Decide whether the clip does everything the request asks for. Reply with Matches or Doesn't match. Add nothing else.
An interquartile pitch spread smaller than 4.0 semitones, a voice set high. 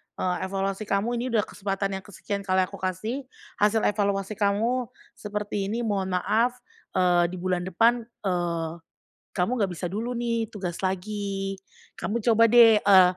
Matches